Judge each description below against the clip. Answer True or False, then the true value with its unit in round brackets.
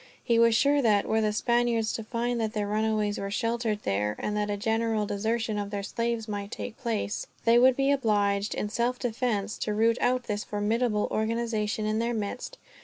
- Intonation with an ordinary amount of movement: False (2.2 semitones)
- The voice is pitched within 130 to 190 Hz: False (220 Hz)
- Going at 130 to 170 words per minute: False (195 wpm)